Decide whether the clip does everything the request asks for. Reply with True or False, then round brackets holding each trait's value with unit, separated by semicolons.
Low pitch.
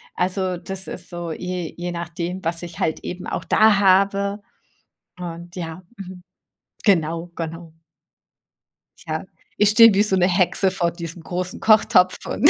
False (180 Hz)